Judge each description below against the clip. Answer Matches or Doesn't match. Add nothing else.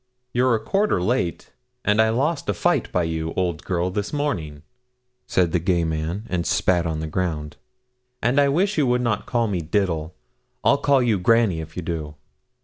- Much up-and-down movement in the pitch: Matches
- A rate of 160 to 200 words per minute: Matches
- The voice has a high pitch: Doesn't match